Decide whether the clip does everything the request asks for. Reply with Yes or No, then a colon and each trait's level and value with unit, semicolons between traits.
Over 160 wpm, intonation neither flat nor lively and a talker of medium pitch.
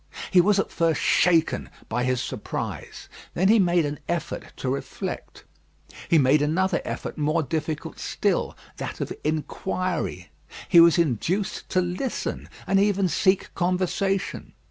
No: average, 140 wpm; average, 3.7 semitones; medium, 170 Hz